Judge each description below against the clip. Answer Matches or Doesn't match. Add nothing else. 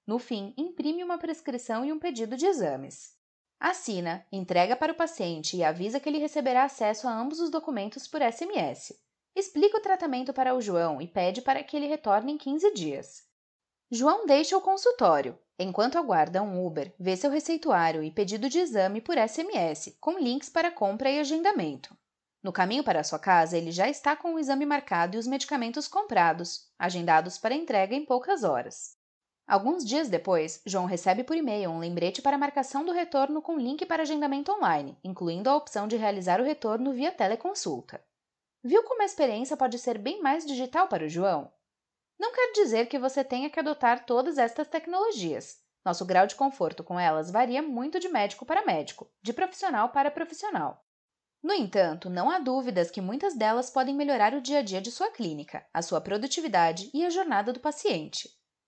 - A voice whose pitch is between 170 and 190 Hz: Doesn't match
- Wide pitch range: Matches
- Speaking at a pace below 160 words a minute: Doesn't match